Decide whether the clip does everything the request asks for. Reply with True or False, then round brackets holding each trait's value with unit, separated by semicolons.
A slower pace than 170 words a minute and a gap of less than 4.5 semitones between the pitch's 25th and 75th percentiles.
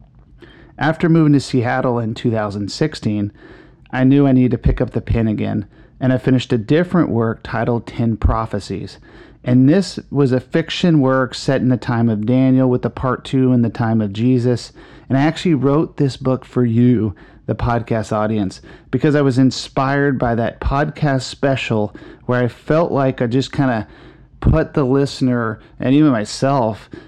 False (175 wpm; 3.3 semitones)